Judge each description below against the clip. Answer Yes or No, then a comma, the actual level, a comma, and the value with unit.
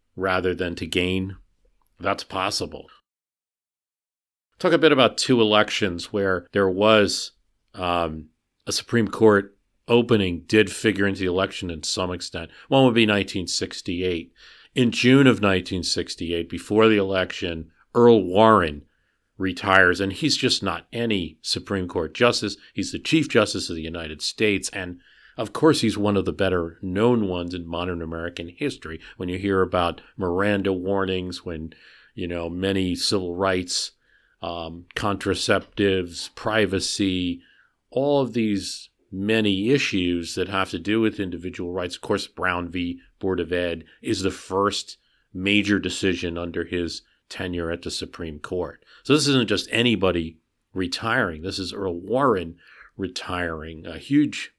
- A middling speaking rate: Yes, average, 145 wpm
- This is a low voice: Yes, very low, 95 Hz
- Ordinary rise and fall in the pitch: Yes, average, 3.3 semitones